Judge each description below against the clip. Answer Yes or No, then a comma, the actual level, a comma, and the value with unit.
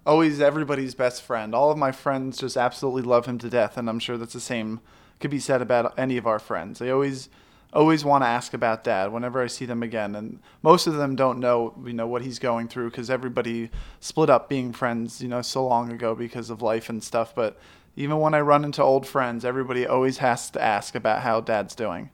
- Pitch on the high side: No, low, 125 Hz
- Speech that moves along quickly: Yes, fast, 235 wpm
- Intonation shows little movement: Yes, narrow, 2.3 semitones